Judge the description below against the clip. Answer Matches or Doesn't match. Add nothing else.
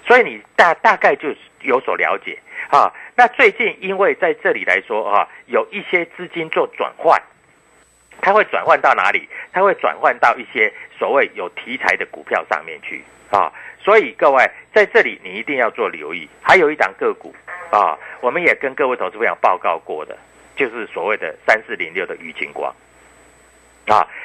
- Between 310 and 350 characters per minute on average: Doesn't match